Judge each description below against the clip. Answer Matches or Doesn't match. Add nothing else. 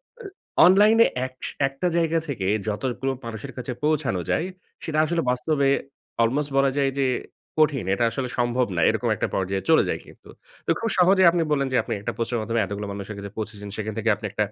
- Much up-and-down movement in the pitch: Matches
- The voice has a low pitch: Matches